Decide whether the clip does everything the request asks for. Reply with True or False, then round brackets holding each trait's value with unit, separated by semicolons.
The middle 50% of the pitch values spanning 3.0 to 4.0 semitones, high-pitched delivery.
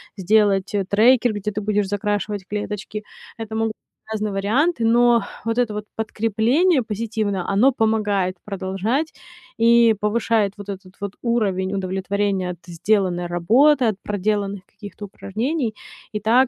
False (2.5 semitones; 210 Hz)